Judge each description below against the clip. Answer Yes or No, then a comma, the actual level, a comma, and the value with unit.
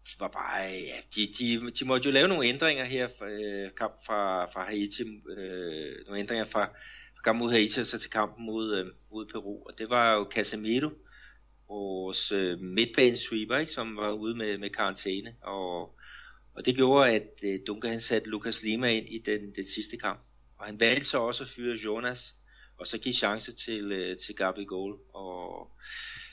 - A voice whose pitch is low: Yes, low, 110 Hz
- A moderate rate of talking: Yes, average, 180 wpm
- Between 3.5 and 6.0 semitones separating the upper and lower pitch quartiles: No, average, 2.8 semitones